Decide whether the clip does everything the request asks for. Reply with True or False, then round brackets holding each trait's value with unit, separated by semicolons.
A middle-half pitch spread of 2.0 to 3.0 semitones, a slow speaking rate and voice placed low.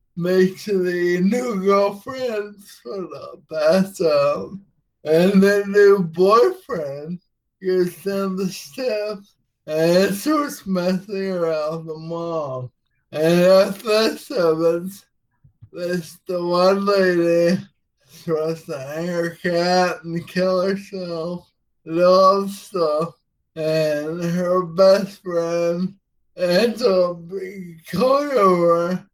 False (2.7 semitones; 100 wpm; 180 Hz)